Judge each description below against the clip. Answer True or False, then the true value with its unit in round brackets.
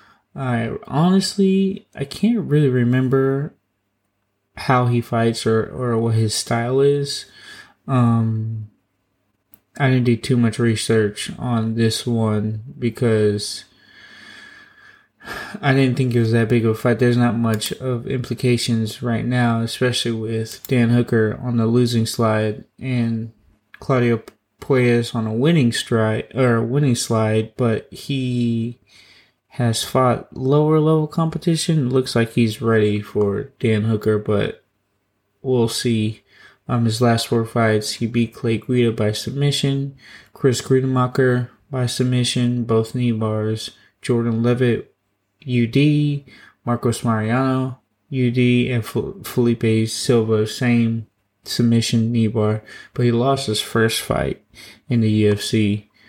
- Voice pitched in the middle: False (120 Hz)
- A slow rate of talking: True (130 wpm)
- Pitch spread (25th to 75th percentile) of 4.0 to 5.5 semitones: False (2.7 semitones)